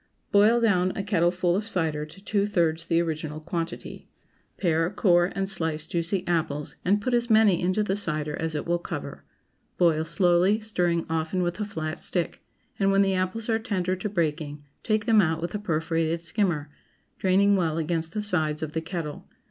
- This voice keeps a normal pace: Yes, average, 185 wpm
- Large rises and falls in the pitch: No, average, 3.6 semitones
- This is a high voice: No, medium, 175 Hz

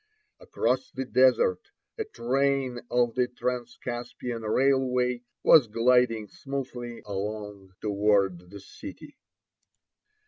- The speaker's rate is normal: No, slow, 95 wpm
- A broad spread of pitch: No, average, 3.3 semitones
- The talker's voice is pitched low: Yes, low, 120 Hz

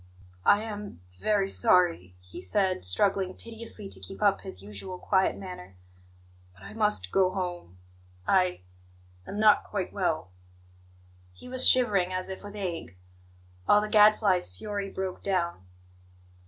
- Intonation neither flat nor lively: Yes, average, 3.3 semitones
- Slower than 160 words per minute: Yes, average, 140 wpm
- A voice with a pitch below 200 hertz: Yes, high, 190 Hz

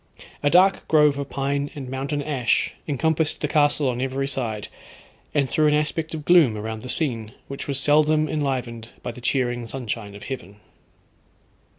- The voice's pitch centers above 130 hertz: Yes, medium, 140 Hz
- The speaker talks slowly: No, average, 170 wpm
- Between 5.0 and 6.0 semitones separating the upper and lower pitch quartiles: No, average, 3.7 semitones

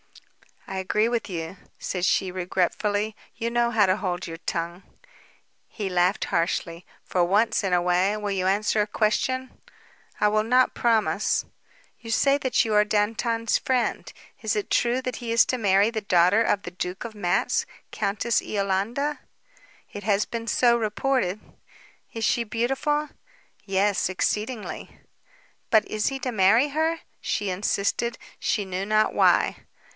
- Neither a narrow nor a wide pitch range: Yes, average, 3.7 semitones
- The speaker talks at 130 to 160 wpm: Yes, average, 155 wpm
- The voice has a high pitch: Yes, high, 210 Hz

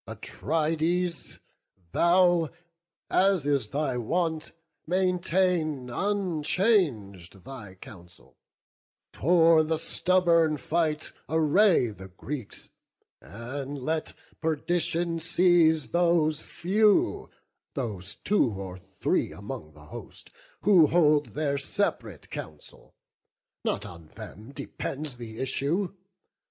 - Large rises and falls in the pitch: Yes, wide, 6.1 semitones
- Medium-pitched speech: Yes, medium, 155 Hz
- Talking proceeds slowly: Yes, slow, 90 wpm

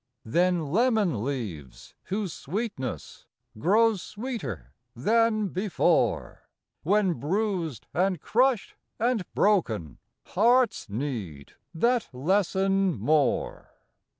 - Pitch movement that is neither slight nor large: No, wide, 8.0 semitones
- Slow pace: Yes, slow, 85 wpm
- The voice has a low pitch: No, medium, 185 Hz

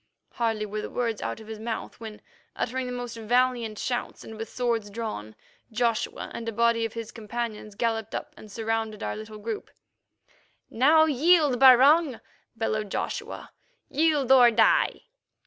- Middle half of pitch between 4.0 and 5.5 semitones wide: No, narrow, 2.4 semitones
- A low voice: No, high, 230 Hz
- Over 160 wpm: No, average, 155 wpm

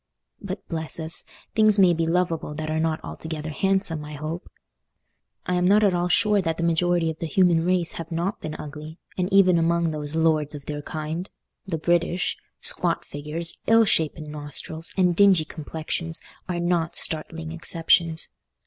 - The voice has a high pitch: No, medium, 165 Hz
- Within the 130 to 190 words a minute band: Yes, average, 170 wpm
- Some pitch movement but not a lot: No, narrow, 2.2 semitones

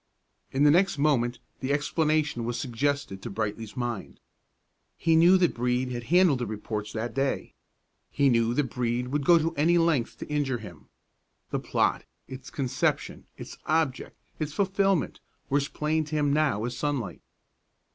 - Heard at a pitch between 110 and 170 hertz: Yes, medium, 140 Hz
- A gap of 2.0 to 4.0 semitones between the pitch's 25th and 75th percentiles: No, average, 4.4 semitones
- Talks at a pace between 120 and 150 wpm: No, average, 160 wpm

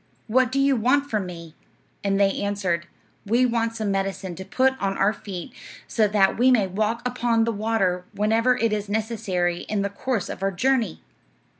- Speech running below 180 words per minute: No, average, 185 wpm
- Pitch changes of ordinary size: Yes, average, 3.2 semitones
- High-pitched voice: Yes, high, 210 Hz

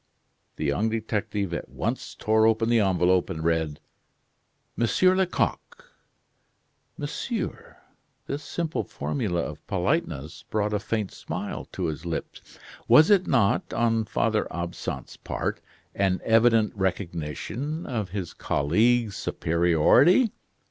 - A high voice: No, low, 105 Hz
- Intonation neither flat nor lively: No, wide, 5.7 semitones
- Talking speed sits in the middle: No, slow, 120 wpm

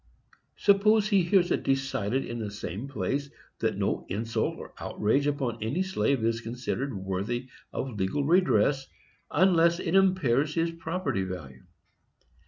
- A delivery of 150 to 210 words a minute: No, average, 140 wpm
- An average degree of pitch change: No, wide, 7.2 semitones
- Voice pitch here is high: No, low, 135 Hz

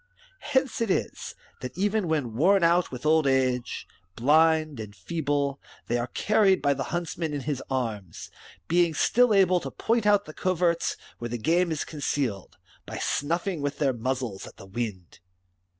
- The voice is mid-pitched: Yes, medium, 150 Hz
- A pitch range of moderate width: No, wide, 5.9 semitones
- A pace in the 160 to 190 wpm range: Yes, average, 170 wpm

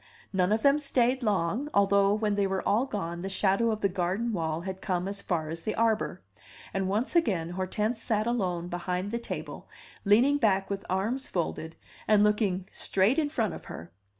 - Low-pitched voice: No, high, 200 Hz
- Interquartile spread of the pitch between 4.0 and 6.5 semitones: No, average, 3.5 semitones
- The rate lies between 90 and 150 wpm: No, average, 190 wpm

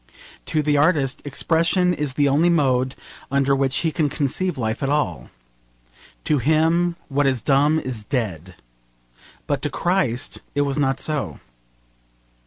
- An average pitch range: Yes, average, 3.2 semitones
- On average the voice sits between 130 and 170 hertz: Yes, medium, 140 Hz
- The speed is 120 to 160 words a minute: Yes, average, 145 wpm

